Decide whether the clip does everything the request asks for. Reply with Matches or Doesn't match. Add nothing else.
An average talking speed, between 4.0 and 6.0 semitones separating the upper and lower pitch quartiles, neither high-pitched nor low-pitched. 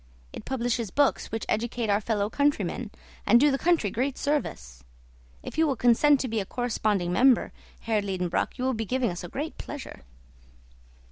Doesn't match